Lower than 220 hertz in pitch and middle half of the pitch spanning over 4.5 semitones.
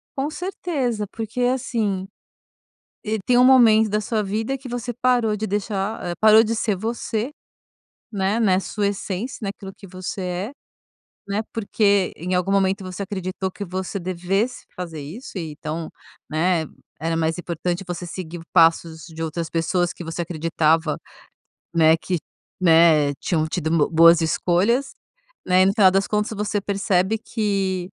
No: high, 190 Hz; average, 4.1 semitones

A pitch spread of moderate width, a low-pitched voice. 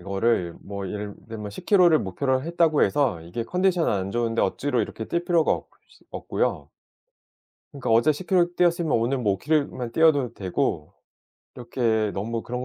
No: wide, 7.2 semitones; low, 120 Hz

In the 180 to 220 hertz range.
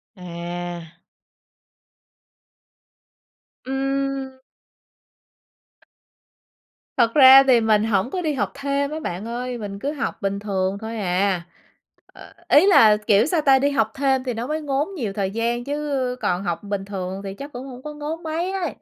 No: high, 245 Hz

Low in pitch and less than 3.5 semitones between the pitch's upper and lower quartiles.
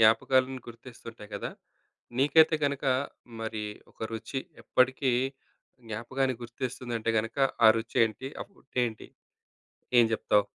Yes: low, 120 Hz; average, 2.8 semitones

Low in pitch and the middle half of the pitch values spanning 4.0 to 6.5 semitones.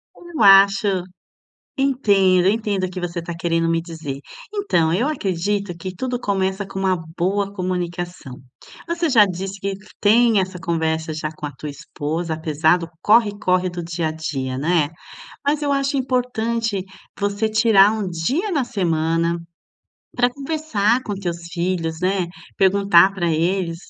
No: high, 190 Hz; average, 4.3 semitones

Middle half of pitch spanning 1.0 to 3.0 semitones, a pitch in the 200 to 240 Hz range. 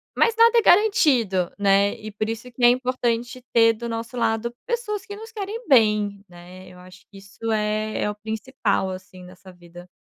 No: average, 4.6 semitones; high, 225 Hz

